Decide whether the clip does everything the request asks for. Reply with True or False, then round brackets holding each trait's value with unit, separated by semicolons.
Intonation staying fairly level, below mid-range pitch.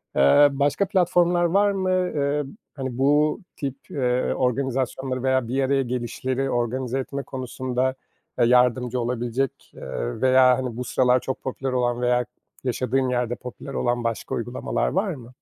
True (1.9 semitones; 130 Hz)